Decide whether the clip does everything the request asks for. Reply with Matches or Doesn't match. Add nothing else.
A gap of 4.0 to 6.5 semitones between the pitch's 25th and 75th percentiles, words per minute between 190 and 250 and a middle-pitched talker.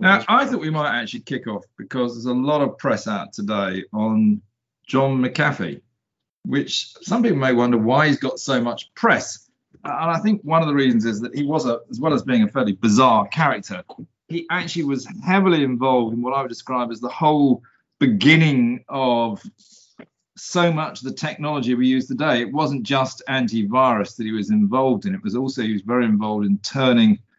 Doesn't match